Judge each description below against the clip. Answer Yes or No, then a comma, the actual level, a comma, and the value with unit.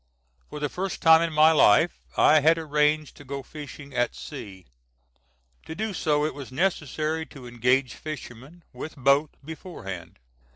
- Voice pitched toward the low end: No, medium, 150 Hz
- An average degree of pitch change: Yes, average, 3.1 semitones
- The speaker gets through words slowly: No, average, 155 wpm